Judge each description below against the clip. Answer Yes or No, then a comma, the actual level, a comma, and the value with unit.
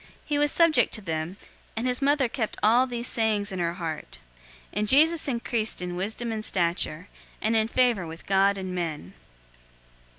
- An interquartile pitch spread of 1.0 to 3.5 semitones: No, wide, 5.4 semitones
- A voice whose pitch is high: Yes, high, 215 Hz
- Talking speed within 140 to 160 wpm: No, average, 175 wpm